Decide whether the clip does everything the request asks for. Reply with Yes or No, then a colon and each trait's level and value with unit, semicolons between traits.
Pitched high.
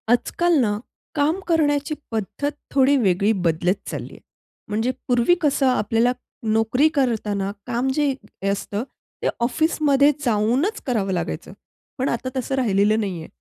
Yes: high, 240 Hz